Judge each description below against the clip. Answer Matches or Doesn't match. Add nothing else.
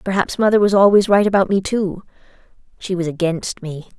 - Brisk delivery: Doesn't match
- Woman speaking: Matches